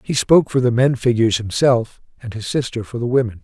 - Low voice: Yes, low, 120 Hz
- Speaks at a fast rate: Yes, fast, 225 wpm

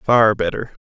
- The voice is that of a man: Yes, male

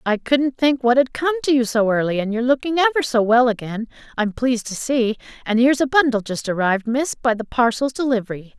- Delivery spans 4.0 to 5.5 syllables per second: No, 6.1 syllables/s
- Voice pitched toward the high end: Yes, high, 245 Hz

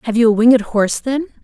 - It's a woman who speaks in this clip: Yes, female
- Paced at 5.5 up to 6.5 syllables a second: No, 7.0 syllables/s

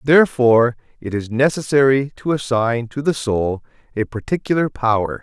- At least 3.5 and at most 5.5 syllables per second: Yes, 5.1 syllables/s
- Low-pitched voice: Yes, low, 125 Hz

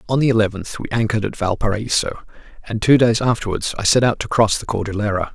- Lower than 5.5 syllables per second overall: No, 6.5 syllables/s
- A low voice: Yes, low, 110 Hz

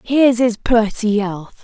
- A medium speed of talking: Yes, average, 145 wpm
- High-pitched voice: Yes, high, 225 Hz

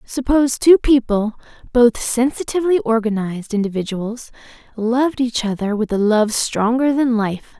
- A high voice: Yes, high, 235 Hz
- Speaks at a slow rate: Yes, slow, 125 wpm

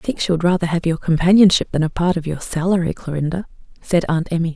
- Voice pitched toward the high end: No, medium, 170 Hz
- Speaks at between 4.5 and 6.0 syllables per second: No, 6.5 syllables/s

